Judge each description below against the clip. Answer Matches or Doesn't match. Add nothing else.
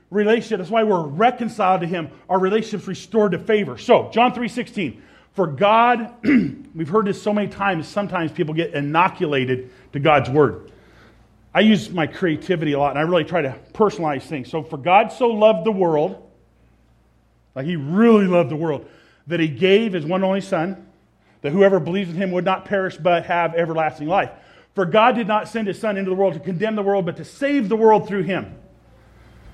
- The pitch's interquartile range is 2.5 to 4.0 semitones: Doesn't match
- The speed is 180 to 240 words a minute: Matches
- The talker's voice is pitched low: Doesn't match